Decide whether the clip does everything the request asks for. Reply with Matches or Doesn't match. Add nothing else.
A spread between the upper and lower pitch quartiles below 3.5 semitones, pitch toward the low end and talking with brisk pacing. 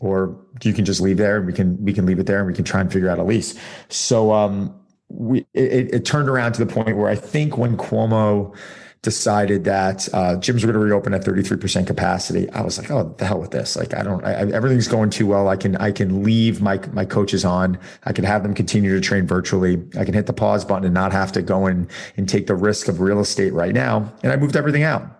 Matches